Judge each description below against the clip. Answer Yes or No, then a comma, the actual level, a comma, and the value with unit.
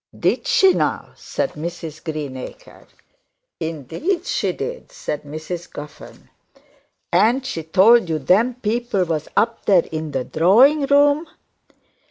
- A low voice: No, medium, 185 Hz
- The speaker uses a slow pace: Yes, slow, 125 wpm